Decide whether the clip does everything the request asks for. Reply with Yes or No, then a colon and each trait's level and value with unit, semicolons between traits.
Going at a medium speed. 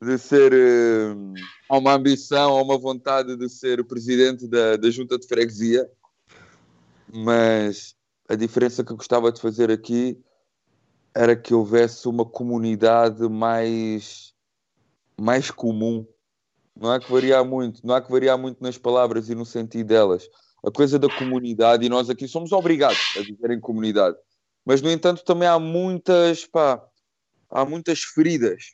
Yes: average, 155 wpm